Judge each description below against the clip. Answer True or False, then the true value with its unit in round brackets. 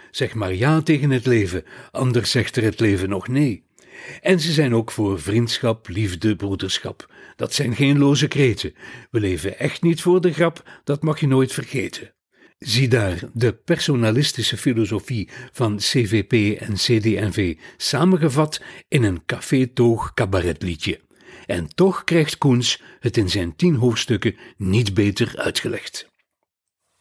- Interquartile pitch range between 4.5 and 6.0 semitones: True (5.3 semitones)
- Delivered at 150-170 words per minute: False (140 wpm)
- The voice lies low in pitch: True (120 Hz)